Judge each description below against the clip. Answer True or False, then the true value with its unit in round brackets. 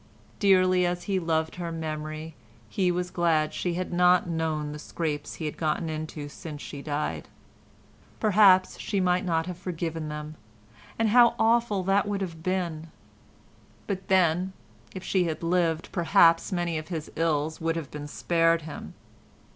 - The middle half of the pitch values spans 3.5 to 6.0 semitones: False (2.8 semitones)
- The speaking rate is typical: True (155 wpm)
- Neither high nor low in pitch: True (165 Hz)